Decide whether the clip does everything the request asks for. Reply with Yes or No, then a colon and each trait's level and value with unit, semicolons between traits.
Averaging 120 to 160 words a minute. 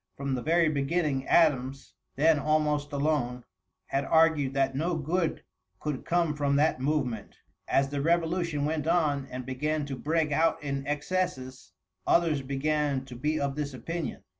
Yes: average, 155 wpm